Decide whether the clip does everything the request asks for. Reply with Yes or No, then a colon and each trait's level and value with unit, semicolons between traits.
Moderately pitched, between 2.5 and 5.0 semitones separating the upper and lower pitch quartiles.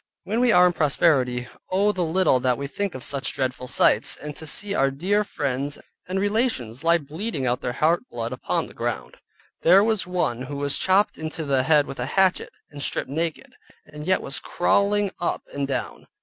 No: medium, 155 Hz; wide, 5.6 semitones